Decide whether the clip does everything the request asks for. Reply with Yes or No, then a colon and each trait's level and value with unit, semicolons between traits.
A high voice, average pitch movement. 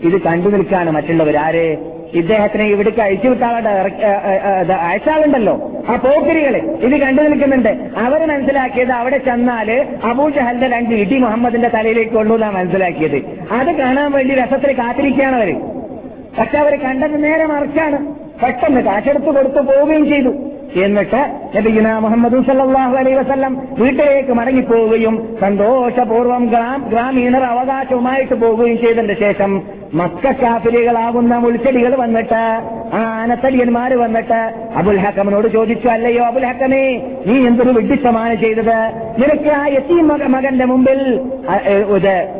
Yes: high, 240 Hz; average, 3.3 semitones